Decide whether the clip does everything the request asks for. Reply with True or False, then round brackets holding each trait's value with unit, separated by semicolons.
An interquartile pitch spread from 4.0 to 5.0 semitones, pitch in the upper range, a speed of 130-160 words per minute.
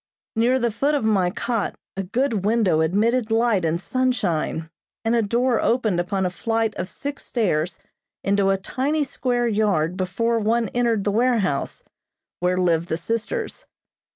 True (4.5 semitones; 220 Hz; 155 wpm)